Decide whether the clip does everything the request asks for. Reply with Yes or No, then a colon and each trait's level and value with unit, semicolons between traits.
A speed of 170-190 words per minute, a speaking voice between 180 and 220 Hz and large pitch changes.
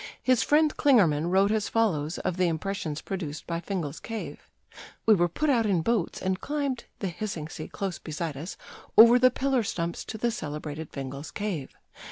Yes: average, 180 wpm; high, 190 Hz; wide, 6.1 semitones